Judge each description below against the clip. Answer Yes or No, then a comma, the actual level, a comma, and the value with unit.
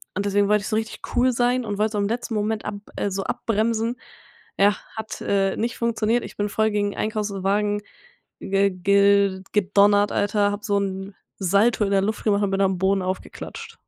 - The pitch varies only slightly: Yes, narrow, 1.6 semitones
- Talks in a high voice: Yes, high, 205 Hz